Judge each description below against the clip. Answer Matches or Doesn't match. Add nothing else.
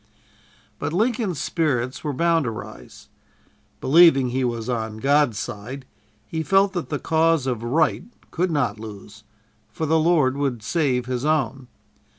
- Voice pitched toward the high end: Doesn't match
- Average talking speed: Matches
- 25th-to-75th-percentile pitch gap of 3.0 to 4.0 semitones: Doesn't match